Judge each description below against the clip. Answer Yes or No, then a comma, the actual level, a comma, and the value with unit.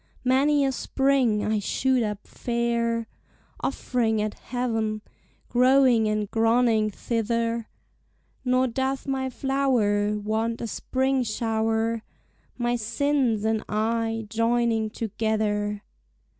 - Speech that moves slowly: Yes, slow, 105 wpm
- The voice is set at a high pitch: Yes, high, 230 Hz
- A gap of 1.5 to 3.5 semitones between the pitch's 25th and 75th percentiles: Yes, narrow, 2.6 semitones